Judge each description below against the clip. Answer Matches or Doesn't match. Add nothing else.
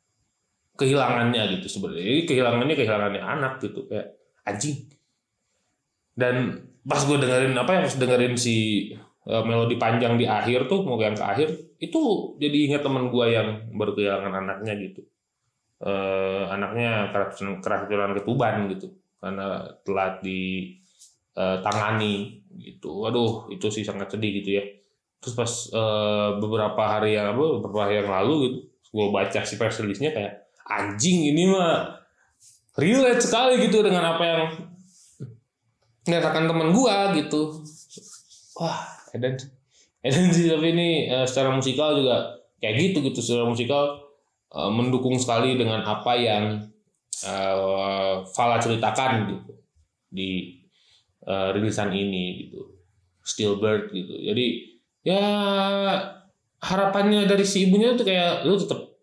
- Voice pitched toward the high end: Doesn't match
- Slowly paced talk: Doesn't match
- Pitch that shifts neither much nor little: Doesn't match